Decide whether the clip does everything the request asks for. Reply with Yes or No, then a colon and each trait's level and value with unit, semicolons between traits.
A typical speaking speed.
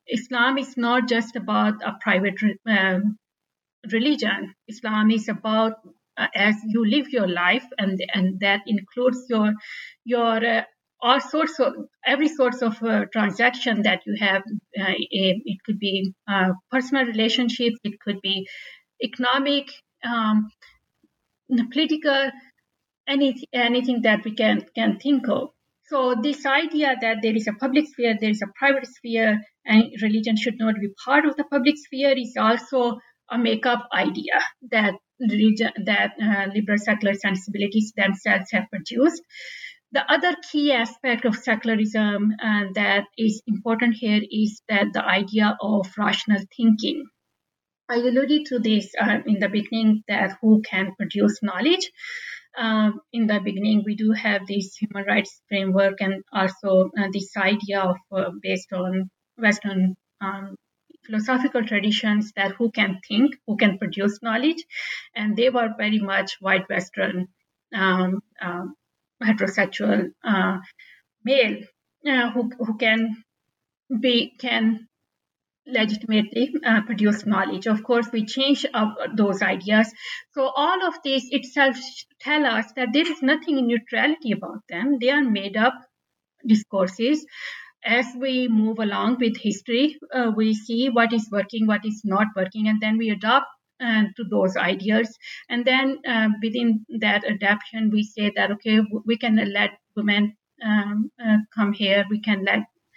Yes: average, 150 wpm